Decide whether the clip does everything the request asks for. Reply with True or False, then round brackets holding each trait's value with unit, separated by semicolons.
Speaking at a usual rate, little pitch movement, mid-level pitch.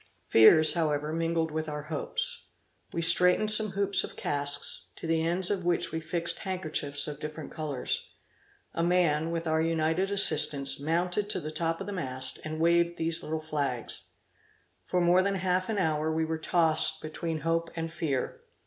True (175 wpm; 2.1 semitones; 165 Hz)